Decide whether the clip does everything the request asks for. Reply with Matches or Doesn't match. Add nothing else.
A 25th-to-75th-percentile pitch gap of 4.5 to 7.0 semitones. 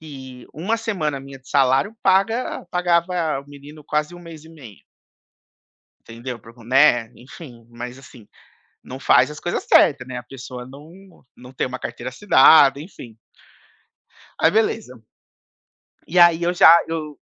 Matches